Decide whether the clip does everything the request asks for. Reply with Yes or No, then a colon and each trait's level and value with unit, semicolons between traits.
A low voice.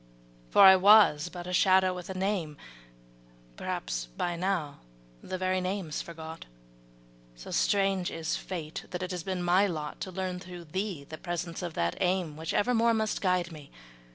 No: medium, 180 Hz